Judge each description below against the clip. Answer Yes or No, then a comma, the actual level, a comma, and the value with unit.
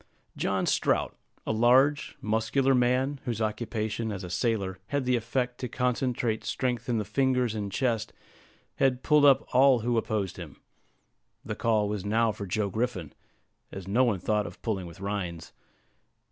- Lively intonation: No, average, 3.4 semitones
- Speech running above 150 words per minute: Yes, average, 160 wpm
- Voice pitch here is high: No, low, 115 Hz